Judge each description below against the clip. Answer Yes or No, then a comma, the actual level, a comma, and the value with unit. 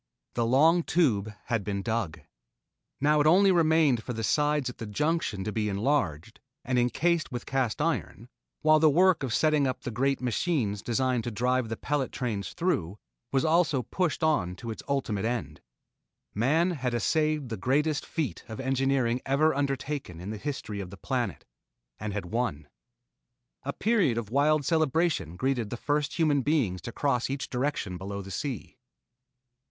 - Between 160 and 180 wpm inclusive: Yes, average, 170 wpm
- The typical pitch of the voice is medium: No, low, 130 Hz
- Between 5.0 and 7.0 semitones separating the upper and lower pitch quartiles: Yes, average, 5.3 semitones